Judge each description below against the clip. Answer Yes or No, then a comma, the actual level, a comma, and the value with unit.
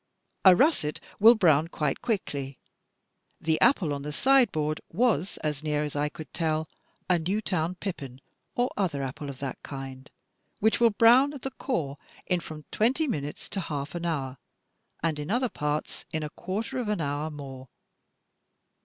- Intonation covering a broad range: Yes, wide, 6.4 semitones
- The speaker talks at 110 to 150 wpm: No, average, 165 wpm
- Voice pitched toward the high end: No, medium, 160 Hz